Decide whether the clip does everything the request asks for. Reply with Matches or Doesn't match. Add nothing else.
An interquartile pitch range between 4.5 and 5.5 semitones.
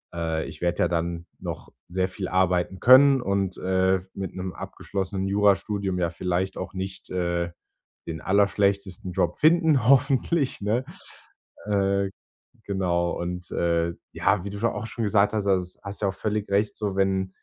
Doesn't match